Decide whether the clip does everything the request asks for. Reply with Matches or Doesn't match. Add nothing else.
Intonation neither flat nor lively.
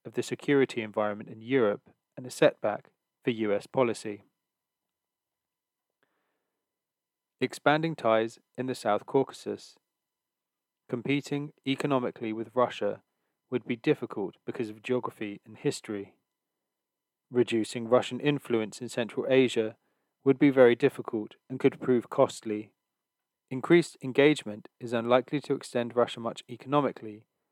Matches